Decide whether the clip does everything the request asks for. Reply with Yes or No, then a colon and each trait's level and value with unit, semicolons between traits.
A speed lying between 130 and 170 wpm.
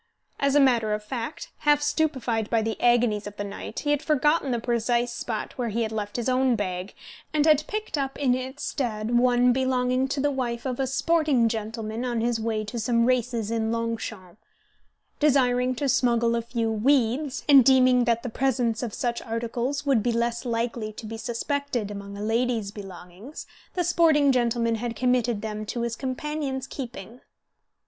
No: average, 185 wpm